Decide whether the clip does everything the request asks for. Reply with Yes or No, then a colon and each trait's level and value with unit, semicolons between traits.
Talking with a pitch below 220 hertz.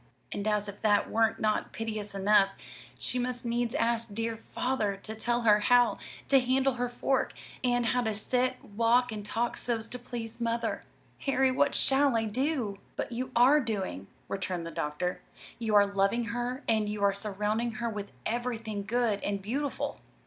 No: high, 230 Hz